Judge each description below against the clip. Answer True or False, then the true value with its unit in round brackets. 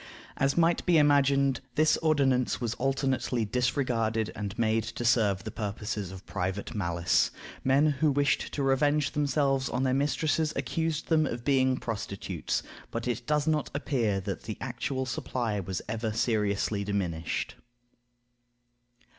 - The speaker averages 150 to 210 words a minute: False (140 wpm)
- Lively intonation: False (4.7 semitones)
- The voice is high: False (125 Hz)